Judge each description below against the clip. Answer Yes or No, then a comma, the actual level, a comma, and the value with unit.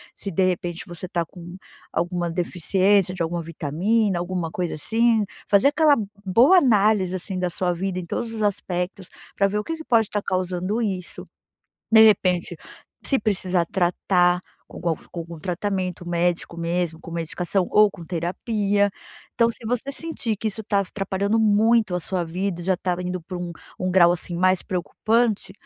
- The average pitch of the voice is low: No, medium, 185 Hz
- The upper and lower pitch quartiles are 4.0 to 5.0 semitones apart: No, average, 3.1 semitones